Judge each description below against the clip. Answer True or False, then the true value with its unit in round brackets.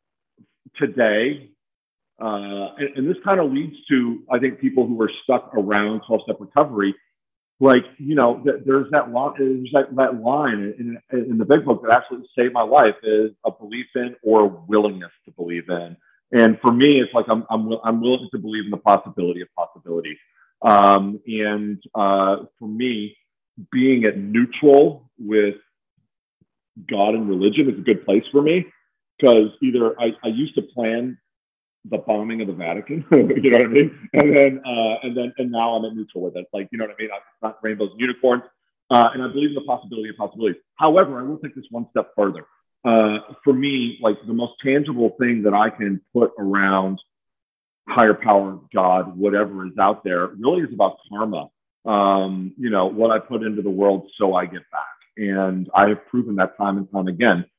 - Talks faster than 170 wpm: True (195 wpm)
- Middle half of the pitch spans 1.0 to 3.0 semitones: False (3.8 semitones)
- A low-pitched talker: True (110 Hz)